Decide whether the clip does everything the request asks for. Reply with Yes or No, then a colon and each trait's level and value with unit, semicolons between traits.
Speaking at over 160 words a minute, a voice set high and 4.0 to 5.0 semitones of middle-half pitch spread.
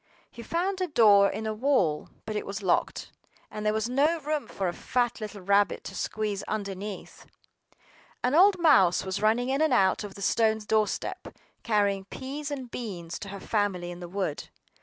Yes: average, 185 wpm; high, 215 Hz; average, 4.4 semitones